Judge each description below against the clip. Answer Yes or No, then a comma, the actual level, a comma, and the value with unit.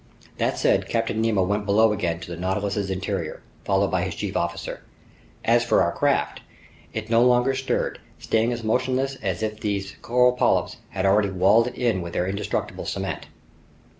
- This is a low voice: Yes, low, 105 Hz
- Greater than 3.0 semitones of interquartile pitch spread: Yes, average, 3.4 semitones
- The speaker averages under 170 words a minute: No, average, 175 wpm